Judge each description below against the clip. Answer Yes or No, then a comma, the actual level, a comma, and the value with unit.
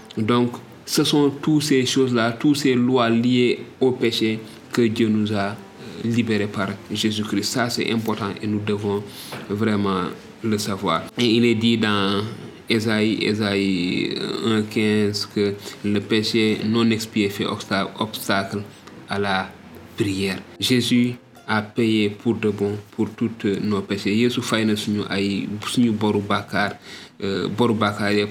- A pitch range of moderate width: No, narrow, 2.3 semitones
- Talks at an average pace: Yes, average, 120 wpm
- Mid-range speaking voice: No, low, 110 Hz